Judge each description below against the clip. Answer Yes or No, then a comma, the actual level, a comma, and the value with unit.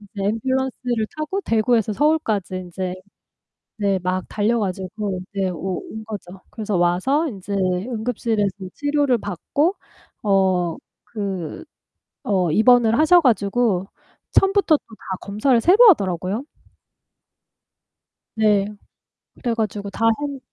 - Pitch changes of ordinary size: Yes, average, 4.6 semitones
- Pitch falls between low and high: No, high, 215 Hz